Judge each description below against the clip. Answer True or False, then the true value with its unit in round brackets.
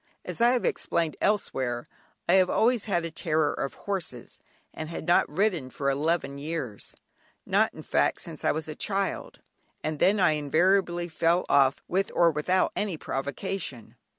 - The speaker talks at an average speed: True (165 wpm)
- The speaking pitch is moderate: True (165 Hz)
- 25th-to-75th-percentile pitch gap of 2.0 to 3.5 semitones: False (4.7 semitones)